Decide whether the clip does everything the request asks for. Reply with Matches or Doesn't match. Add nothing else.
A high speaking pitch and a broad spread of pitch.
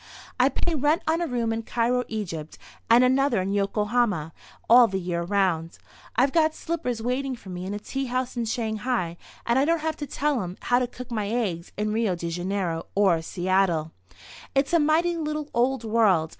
Matches